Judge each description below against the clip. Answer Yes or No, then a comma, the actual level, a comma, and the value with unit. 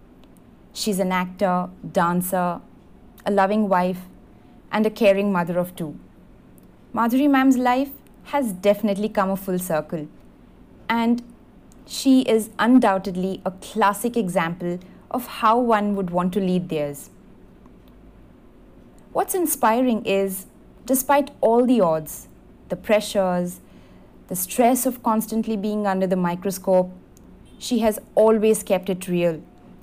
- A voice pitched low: No, high, 200 Hz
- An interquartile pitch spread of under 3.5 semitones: No, average, 4.0 semitones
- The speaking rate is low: No, average, 120 wpm